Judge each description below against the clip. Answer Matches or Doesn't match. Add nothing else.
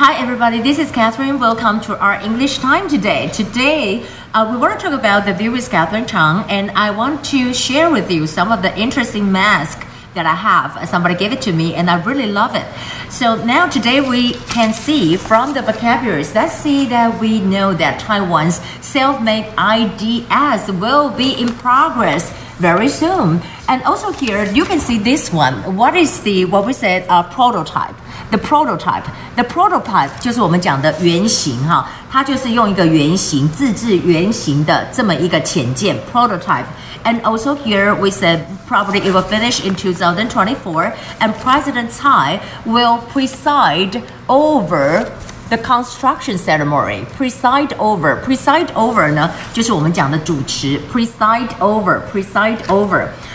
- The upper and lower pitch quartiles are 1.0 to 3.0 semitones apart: Doesn't match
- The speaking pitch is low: Doesn't match